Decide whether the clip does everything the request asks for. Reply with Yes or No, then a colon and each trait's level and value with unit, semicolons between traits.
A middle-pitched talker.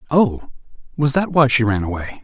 No: low, 130 Hz